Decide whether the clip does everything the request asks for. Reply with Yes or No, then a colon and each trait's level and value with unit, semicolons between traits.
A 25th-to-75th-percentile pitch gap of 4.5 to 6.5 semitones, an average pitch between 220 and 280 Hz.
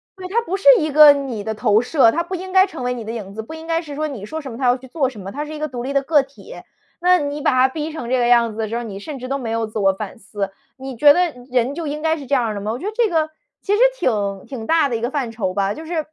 Yes: wide, 5.6 semitones; very high, 265 Hz